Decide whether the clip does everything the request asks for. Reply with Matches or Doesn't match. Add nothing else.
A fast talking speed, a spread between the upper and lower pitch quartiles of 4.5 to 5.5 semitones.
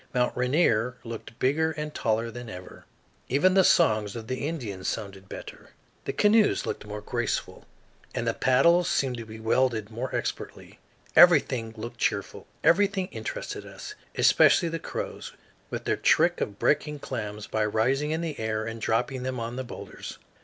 Doesn't match